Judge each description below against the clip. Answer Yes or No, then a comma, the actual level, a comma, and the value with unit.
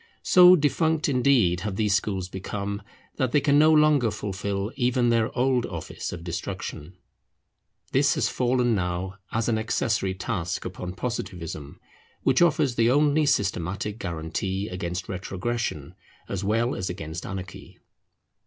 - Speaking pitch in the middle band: No, low, 105 Hz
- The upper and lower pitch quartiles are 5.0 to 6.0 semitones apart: Yes, wide, 5.5 semitones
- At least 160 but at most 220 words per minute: No, slow, 135 wpm